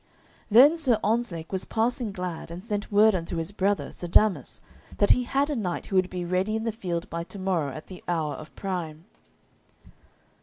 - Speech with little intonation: No, average, 4.3 semitones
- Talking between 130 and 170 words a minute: No, average, 195 wpm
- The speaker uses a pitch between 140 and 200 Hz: Yes, high, 190 Hz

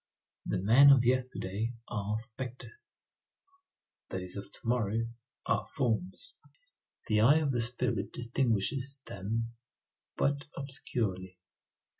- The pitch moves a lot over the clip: No, average, 3.9 semitones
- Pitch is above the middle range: No, low, 115 Hz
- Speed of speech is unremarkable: No, slow, 105 wpm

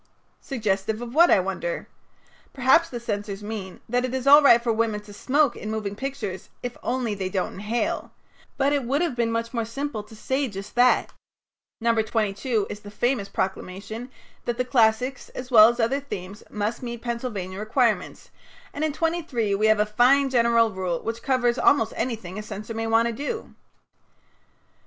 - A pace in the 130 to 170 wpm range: No, average, 185 wpm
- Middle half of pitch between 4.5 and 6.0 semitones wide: No, average, 3.4 semitones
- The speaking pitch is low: No, high, 230 Hz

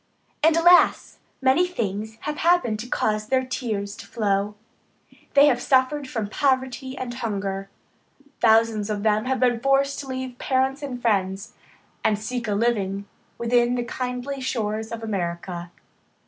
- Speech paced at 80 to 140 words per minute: No, average, 150 wpm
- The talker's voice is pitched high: Yes, high, 235 Hz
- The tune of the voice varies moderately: Yes, average, 3.8 semitones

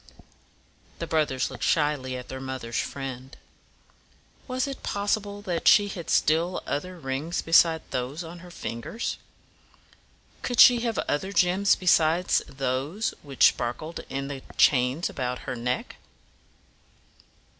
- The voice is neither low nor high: Yes, medium, 155 Hz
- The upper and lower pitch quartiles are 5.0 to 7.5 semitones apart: Yes, wide, 5.6 semitones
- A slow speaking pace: Yes, slow, 125 wpm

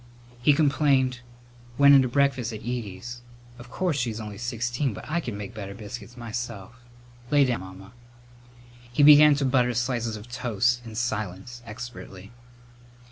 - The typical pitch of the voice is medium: No, low, 120 Hz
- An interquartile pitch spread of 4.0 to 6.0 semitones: No, average, 3.3 semitones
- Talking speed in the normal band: Yes, average, 150 wpm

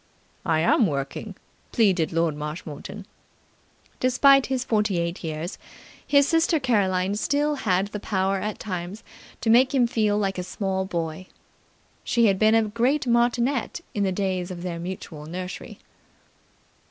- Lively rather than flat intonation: No, average, 4.9 semitones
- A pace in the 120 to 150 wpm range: Yes, average, 145 wpm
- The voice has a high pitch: Yes, high, 195 Hz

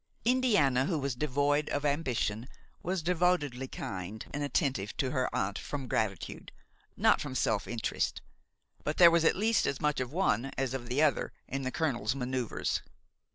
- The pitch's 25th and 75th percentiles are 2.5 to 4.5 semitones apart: Yes, average, 3.9 semitones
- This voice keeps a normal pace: Yes, average, 165 wpm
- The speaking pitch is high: No, low, 135 Hz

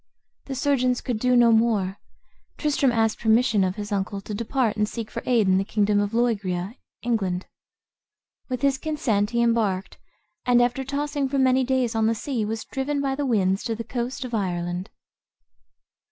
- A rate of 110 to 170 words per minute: No, average, 180 wpm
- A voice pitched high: Yes, high, 230 Hz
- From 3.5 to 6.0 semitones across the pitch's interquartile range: Yes, average, 3.9 semitones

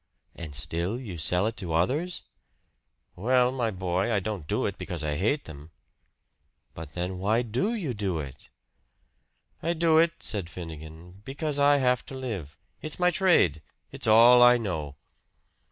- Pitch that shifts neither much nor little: No, wide, 7.6 semitones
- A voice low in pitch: Yes, low, 105 Hz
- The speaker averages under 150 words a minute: No, average, 160 wpm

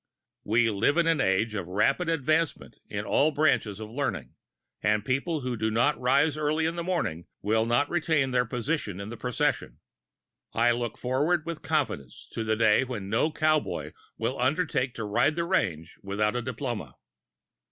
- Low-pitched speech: Yes, low, 125 Hz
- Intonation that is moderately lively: No, wide, 6.1 semitones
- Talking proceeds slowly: No, average, 175 wpm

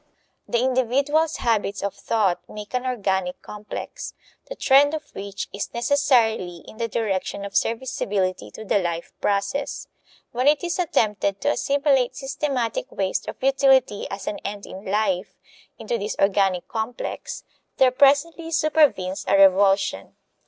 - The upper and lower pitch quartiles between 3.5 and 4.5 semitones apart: No, wide, 5.5 semitones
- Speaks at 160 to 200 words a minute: No, average, 140 wpm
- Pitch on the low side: No, high, 220 Hz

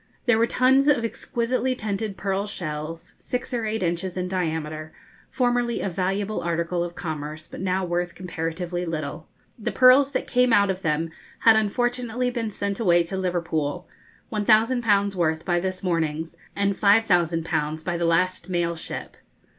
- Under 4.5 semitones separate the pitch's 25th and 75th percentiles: No, average, 4.8 semitones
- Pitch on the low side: No, medium, 185 Hz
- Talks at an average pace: Yes, average, 155 wpm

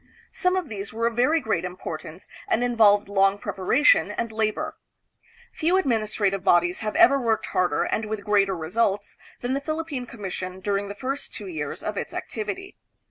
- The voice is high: Yes, high, 215 Hz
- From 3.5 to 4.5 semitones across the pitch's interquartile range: Yes, average, 4.1 semitones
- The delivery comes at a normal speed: Yes, average, 170 wpm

